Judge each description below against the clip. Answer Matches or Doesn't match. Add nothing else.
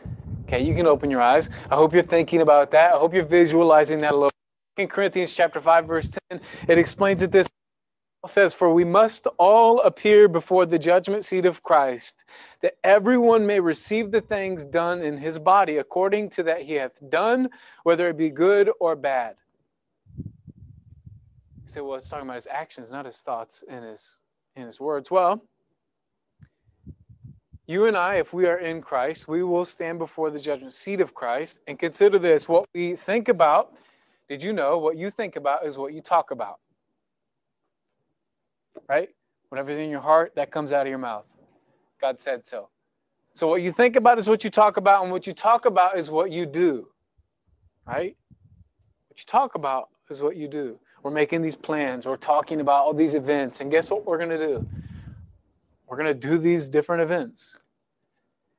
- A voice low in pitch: Doesn't match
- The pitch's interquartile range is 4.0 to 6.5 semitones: Matches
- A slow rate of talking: Doesn't match